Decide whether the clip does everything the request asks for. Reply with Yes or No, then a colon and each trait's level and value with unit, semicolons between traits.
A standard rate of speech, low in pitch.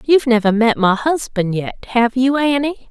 No: average, 185 wpm; high, 245 Hz